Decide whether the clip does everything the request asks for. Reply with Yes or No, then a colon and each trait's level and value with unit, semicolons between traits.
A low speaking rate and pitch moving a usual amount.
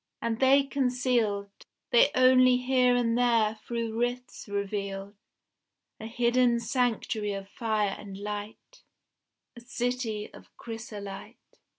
Yes: slow, 110 wpm; average, 3.1 semitones